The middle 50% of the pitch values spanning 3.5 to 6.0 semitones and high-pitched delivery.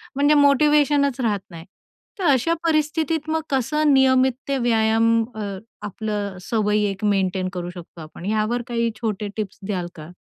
Yes: wide, 5.6 semitones; high, 230 Hz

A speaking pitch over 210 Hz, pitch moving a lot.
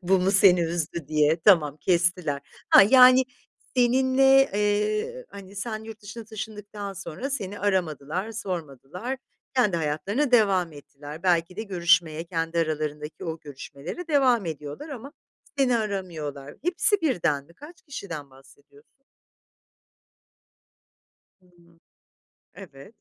No: medium, 185 Hz; wide, 6.2 semitones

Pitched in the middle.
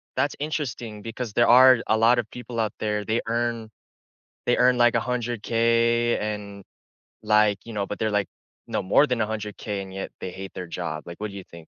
No: low, 110 Hz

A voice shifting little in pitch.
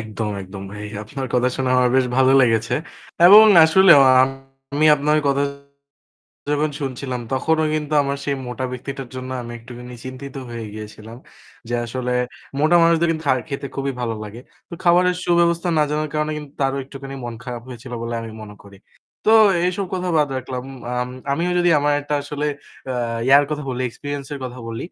No: average, 3.7 semitones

